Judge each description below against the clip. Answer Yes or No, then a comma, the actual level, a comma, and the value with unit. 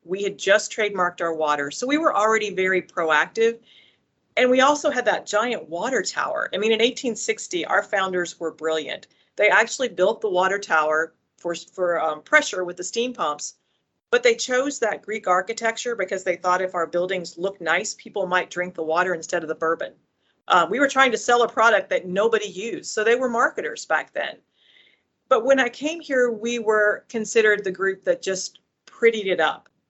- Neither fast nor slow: Yes, average, 195 wpm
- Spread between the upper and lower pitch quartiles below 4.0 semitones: No, average, 4.9 semitones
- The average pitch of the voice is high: Yes, high, 205 Hz